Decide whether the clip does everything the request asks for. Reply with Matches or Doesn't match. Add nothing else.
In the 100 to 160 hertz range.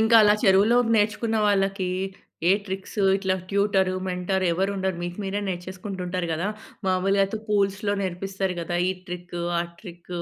Doesn't match